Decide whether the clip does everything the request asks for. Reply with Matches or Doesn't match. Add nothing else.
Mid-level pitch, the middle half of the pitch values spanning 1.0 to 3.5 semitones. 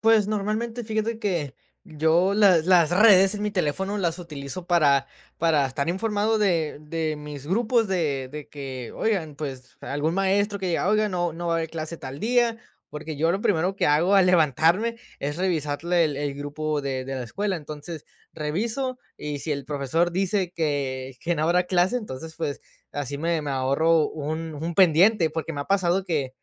Doesn't match